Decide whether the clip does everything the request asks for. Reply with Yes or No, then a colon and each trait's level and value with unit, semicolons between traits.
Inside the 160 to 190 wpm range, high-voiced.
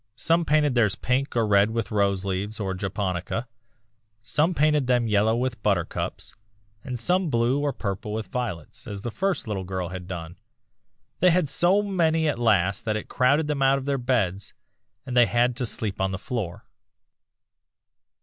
No: average, 170 wpm; low, 115 Hz